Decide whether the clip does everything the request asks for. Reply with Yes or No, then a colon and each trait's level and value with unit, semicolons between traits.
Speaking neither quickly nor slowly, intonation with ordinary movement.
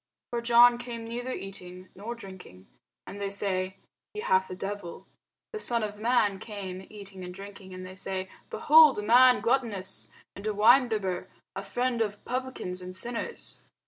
Yes: average, 165 wpm; average, 4.1 semitones